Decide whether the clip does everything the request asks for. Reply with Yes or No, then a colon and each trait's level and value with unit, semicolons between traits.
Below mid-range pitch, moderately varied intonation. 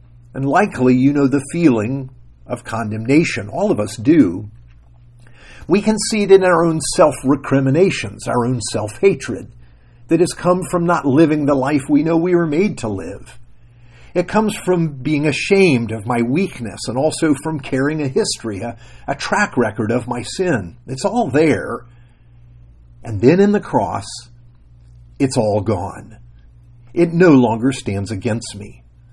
No: low, 125 Hz; wide, 5.7 semitones